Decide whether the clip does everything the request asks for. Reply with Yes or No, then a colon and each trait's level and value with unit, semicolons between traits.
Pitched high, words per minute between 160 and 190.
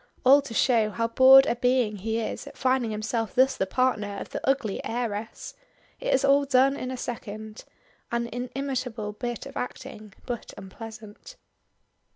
Yes: high, 240 Hz; average, 165 wpm